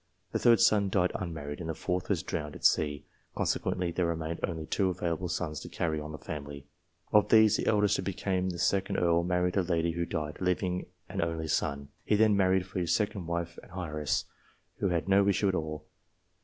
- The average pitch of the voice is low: Yes, very low, 90 Hz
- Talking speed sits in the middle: No, fast, 210 wpm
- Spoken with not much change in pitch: No, average, 3.0 semitones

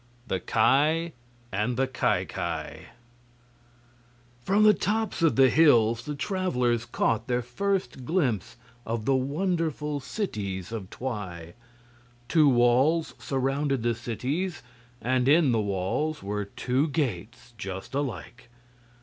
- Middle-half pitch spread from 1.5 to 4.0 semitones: No, average, 5.1 semitones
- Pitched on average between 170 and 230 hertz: No, low, 130 Hz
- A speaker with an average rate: No, slow, 120 wpm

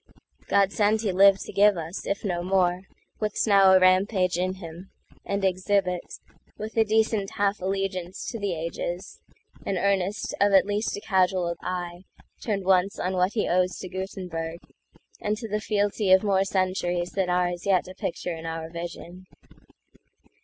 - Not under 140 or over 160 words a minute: Yes, average, 155 wpm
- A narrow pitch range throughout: Yes, narrow, 2.0 semitones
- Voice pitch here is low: No, high, 190 Hz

